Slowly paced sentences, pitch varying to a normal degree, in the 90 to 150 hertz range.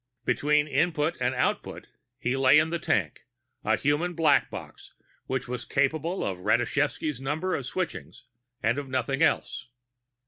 No: average, 145 wpm; average, 3.8 semitones; medium, 140 Hz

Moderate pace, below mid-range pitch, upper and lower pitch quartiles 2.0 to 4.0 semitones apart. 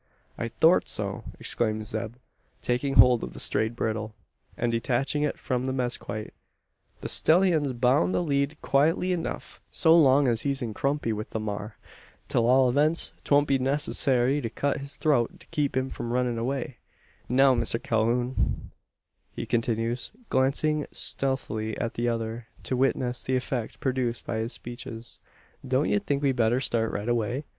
Yes: average, 165 wpm; low, 125 Hz; average, 3.2 semitones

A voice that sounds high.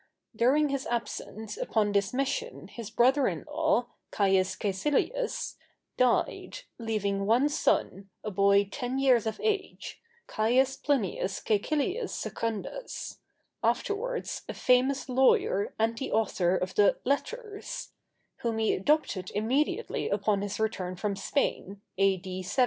Yes: high, 230 Hz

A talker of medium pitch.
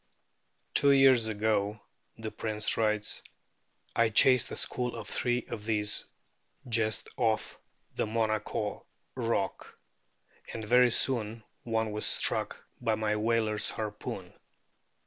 No: low, 110 Hz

